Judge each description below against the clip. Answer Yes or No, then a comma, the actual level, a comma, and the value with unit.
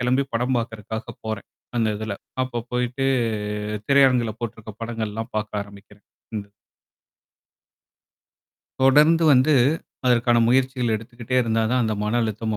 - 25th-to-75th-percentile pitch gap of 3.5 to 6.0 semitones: No, narrow, 2.4 semitones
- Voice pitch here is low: Yes, low, 120 Hz